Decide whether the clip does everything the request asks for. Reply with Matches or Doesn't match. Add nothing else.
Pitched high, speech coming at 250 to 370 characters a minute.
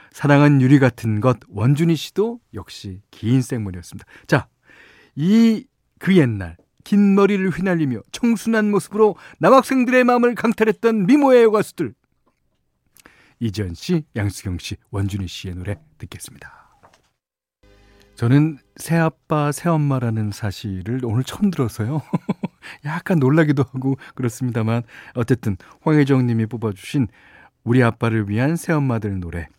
Doesn't match